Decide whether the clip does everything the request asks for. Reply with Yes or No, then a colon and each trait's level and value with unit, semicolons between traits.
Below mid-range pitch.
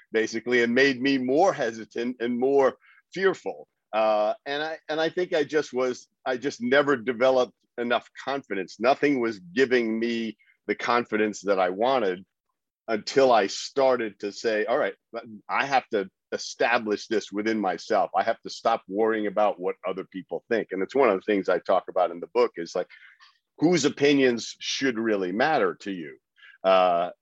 Yes: low, 120 Hz